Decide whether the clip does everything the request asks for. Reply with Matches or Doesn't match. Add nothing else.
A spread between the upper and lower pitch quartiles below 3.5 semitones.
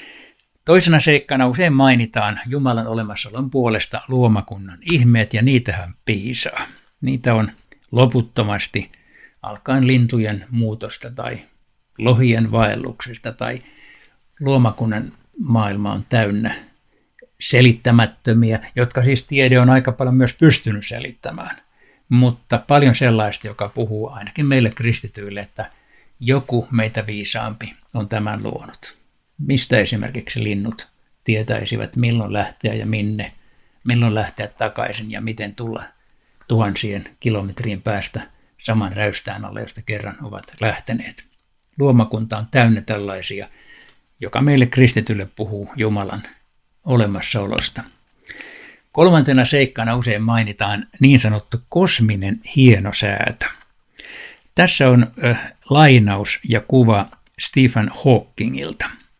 Matches